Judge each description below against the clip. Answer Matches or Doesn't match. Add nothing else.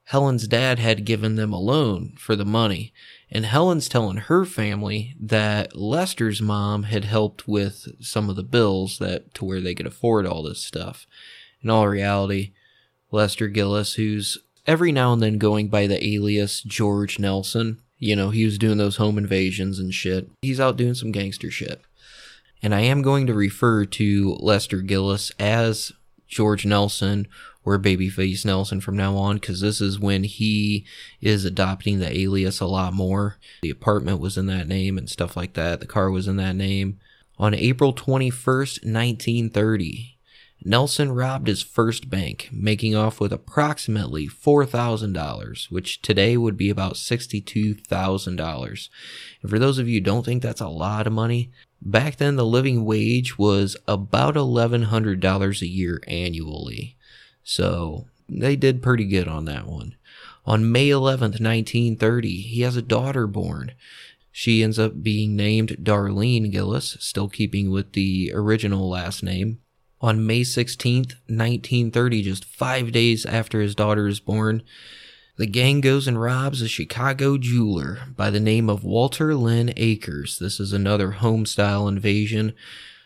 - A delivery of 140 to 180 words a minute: Matches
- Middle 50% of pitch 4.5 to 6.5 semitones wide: Doesn't match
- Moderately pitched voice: Doesn't match